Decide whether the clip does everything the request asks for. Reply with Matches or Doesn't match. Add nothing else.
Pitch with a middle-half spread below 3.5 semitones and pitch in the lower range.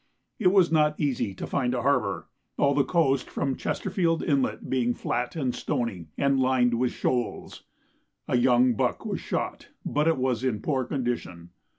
Matches